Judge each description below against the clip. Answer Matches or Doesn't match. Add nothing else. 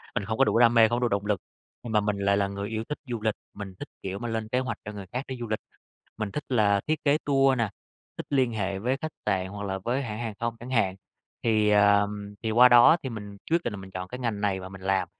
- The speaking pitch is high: Doesn't match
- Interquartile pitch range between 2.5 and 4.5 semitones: Matches